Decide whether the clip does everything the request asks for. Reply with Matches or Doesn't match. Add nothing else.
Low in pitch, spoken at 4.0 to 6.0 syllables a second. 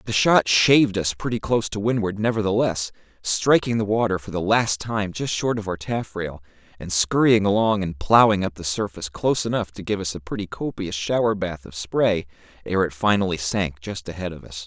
Matches